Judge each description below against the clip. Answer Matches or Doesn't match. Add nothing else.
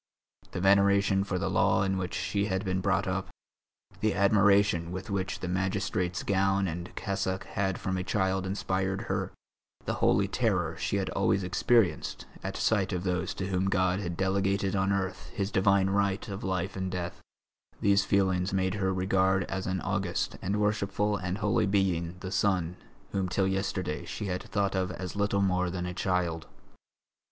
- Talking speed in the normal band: Matches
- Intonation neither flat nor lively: Doesn't match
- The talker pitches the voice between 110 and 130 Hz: Doesn't match